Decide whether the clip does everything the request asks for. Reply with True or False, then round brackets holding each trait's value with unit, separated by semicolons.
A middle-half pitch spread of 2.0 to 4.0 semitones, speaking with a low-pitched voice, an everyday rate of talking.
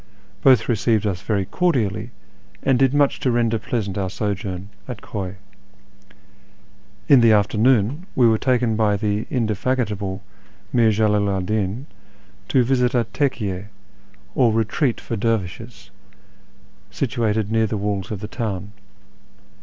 False (3.3 semitones; 110 Hz; 130 wpm)